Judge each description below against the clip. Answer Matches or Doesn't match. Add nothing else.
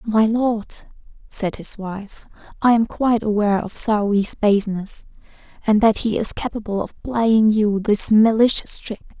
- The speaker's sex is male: Doesn't match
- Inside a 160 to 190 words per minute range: Doesn't match